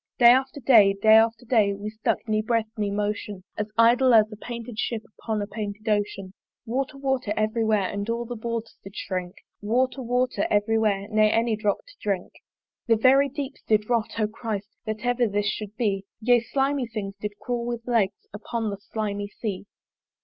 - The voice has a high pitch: Yes, high, 220 Hz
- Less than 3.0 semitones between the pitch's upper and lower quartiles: Yes, narrow, 2.5 semitones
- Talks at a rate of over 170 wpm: Yes, average, 190 wpm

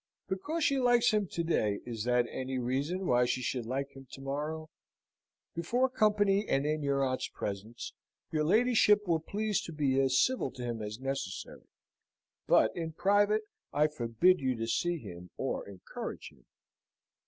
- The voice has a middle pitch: Yes, medium, 150 Hz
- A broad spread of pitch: Yes, wide, 7.9 semitones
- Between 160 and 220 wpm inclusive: Yes, average, 165 wpm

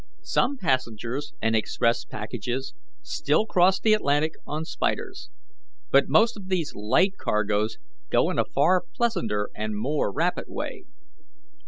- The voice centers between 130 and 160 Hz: Yes, medium, 140 Hz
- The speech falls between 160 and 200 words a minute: No, slow, 135 wpm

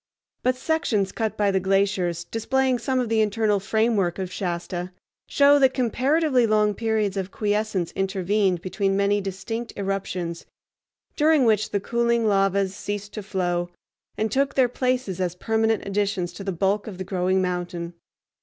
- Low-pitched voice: No, high, 205 Hz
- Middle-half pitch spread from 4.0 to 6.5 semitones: No, average, 3.2 semitones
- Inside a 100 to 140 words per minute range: No, average, 155 wpm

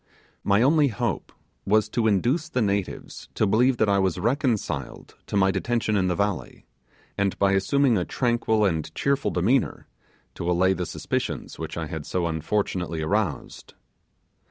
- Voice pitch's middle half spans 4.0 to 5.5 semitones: Yes, average, 4.9 semitones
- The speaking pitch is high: No, low, 100 Hz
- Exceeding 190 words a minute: No, average, 155 wpm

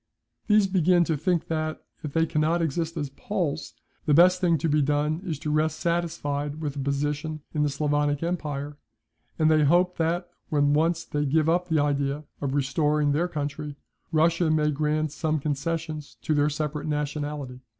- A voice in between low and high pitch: Yes, medium, 155 Hz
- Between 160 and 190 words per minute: Yes, average, 175 wpm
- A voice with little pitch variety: Yes, narrow, 2.1 semitones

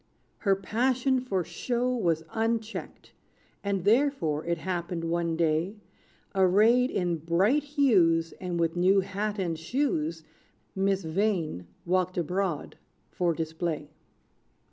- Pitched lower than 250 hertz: Yes, medium, 185 Hz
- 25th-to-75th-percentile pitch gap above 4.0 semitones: Yes, average, 4.8 semitones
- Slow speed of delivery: Yes, slow, 115 wpm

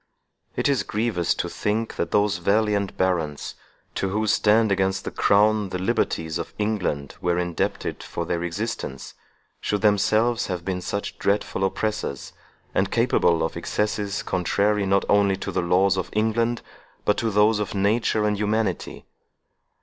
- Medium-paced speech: Yes, average, 150 wpm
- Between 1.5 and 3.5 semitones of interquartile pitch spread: Yes, average, 2.7 semitones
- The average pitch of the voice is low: Yes, low, 100 Hz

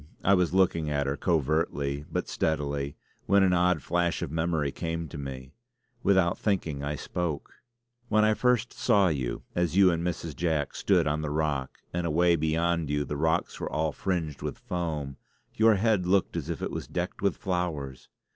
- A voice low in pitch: Yes, very low, 80 Hz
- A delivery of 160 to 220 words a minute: Yes, average, 185 wpm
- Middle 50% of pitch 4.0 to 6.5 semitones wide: No, average, 3.5 semitones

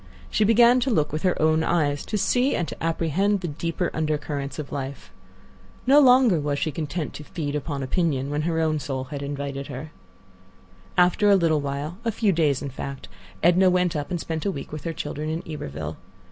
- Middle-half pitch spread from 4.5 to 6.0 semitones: No, average, 3.9 semitones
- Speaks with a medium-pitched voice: Yes, medium, 155 Hz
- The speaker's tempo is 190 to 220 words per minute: Yes, average, 200 wpm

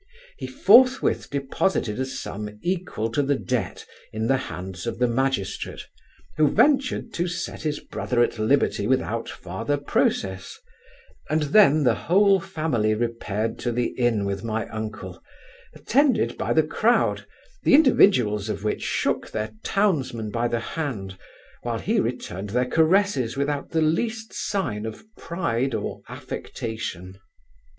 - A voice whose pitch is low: Yes, low, 125 Hz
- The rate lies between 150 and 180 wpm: No, average, 140 wpm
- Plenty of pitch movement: Yes, wide, 7.0 semitones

